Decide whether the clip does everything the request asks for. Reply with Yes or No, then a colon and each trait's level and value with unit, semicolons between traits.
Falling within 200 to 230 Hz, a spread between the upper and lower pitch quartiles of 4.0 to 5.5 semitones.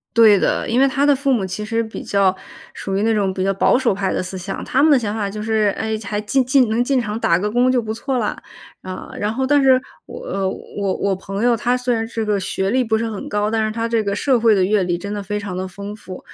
No: high, 215 Hz; average, 3.4 semitones